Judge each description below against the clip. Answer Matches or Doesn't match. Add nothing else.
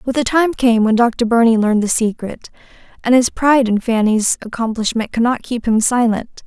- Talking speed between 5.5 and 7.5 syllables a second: Doesn't match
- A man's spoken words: Doesn't match